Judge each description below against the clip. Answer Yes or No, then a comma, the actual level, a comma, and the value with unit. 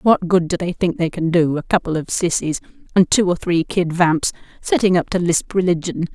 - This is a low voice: No, medium, 180 Hz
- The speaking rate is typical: No, fast, 225 wpm